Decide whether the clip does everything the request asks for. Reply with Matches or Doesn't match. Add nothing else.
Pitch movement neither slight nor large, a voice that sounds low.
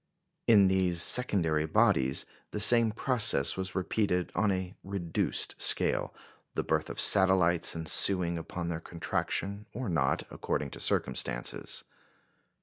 Matches